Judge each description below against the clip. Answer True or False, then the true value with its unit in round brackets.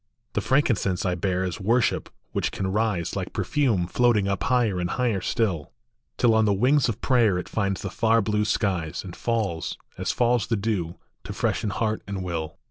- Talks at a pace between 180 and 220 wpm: True (190 wpm)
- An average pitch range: True (4.0 semitones)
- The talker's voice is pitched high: False (105 Hz)